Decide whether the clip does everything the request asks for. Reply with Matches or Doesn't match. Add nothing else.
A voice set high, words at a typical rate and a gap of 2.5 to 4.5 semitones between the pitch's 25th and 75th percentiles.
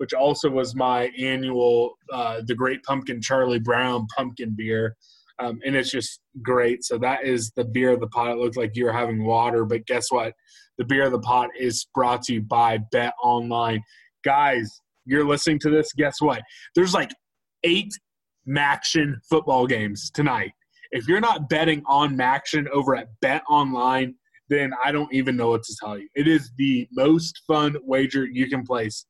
Doesn't match